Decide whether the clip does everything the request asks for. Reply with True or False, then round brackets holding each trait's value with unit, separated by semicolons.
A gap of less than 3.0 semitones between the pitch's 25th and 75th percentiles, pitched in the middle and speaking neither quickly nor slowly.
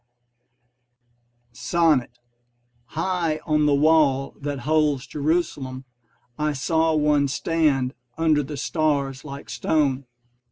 False (2.5 semitones; 150 Hz; 95 wpm)